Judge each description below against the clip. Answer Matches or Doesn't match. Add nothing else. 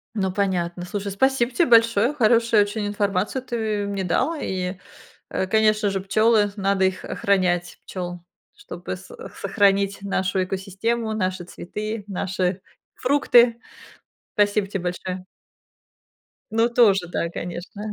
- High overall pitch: Matches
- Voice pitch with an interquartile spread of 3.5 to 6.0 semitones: Doesn't match